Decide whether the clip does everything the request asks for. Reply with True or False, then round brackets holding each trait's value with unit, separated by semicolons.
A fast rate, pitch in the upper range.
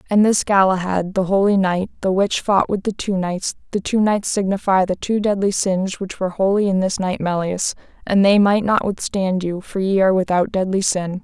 True (215 wpm; 195 Hz)